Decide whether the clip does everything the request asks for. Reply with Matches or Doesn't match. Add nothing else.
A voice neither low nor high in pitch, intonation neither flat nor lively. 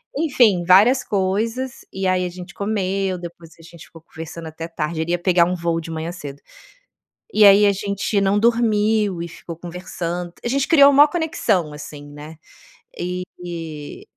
Matches